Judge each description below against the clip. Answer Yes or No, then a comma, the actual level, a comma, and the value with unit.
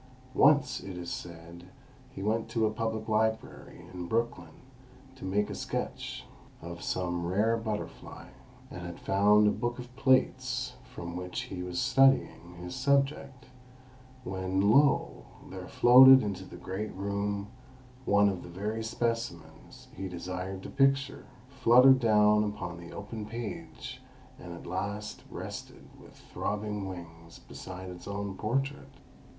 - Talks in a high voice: No, low, 100 Hz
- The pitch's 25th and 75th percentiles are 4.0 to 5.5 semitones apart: Yes, average, 4.3 semitones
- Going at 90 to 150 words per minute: Yes, average, 140 wpm